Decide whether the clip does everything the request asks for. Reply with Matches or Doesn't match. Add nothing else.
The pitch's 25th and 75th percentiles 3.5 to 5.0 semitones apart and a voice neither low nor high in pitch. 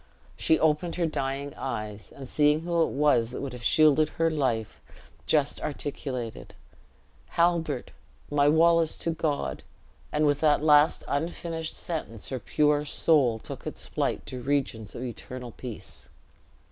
Matches